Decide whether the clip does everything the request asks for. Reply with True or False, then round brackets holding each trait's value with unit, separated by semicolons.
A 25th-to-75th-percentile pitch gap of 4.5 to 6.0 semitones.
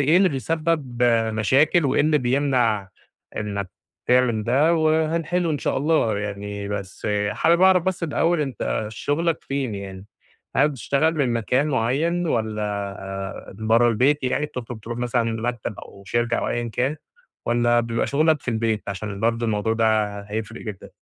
True (5.6 semitones)